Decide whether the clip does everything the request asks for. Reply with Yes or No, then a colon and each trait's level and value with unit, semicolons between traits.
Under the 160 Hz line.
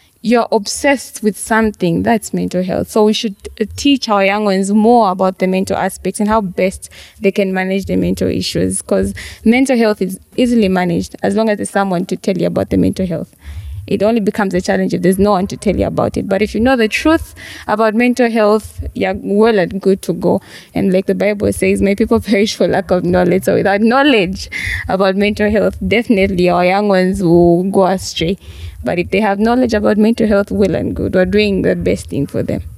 No: high, 200 Hz